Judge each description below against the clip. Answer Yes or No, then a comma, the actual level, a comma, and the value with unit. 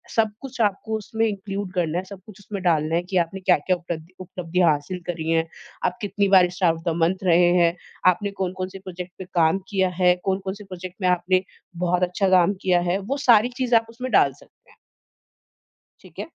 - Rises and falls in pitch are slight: Yes, narrow, 2.2 semitones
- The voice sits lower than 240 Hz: Yes, medium, 185 Hz